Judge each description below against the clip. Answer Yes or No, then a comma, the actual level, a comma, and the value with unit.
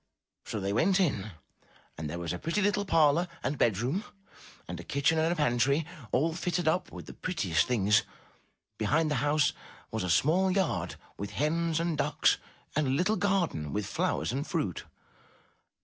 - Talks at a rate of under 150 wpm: No, average, 175 wpm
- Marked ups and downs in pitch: Yes, wide, 7.7 semitones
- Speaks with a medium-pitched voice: Yes, medium, 150 Hz